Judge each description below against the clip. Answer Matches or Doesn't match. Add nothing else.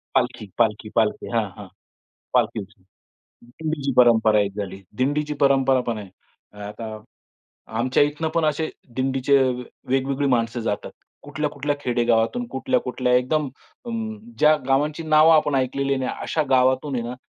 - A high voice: Doesn't match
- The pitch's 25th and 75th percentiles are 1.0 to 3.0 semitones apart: Doesn't match